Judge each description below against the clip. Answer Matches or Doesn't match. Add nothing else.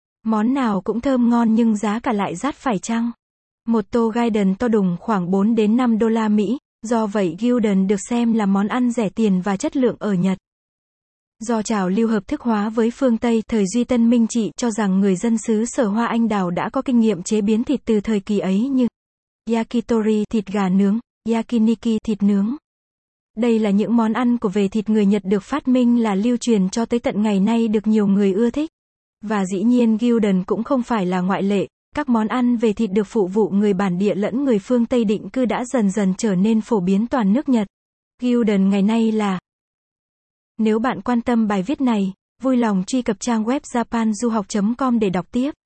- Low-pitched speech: Doesn't match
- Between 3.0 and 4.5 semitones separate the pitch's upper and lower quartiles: Doesn't match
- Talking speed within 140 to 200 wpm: Doesn't match